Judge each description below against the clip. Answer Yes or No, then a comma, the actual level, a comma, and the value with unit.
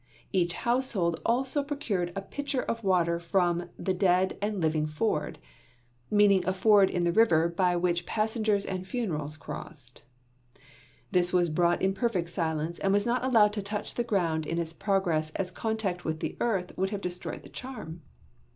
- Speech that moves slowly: No, average, 170 wpm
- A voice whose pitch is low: No, medium, 185 Hz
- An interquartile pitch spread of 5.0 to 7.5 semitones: No, average, 3.9 semitones